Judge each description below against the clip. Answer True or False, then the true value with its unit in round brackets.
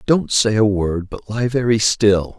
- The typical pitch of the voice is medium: False (110 Hz)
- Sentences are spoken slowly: False (200 wpm)